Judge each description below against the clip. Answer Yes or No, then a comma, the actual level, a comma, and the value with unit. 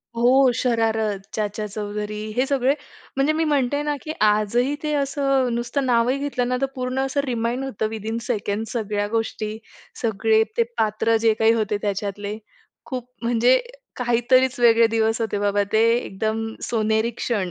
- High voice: Yes, high, 230 Hz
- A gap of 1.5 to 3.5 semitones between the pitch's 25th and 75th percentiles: Yes, average, 3.0 semitones